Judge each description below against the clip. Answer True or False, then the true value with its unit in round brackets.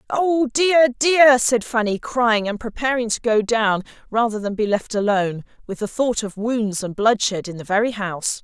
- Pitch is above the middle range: True (225 Hz)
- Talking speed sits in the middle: True (190 wpm)